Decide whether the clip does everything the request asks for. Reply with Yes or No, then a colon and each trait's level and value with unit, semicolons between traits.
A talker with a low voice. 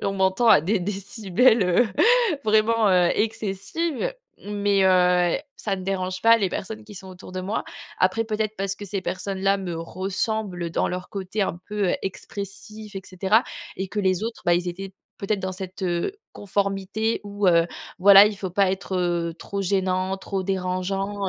No: high, 195 Hz